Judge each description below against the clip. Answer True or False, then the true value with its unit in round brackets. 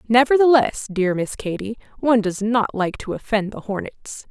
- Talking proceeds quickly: False (165 wpm)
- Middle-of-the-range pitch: False (220 Hz)